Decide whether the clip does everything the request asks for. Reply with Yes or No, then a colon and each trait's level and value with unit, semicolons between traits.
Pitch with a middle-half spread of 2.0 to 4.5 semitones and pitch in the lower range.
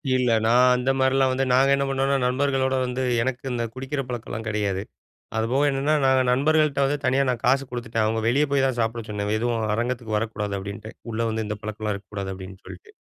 Yes: average, 3.6 semitones; low, 125 Hz